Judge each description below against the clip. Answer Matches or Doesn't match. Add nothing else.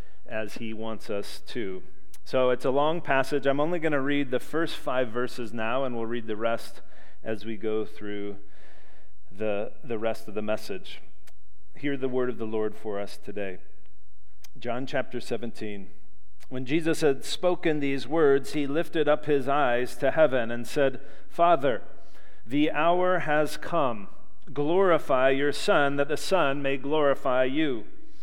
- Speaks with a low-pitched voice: Matches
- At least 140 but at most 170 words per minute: Matches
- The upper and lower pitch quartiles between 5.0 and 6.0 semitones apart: Matches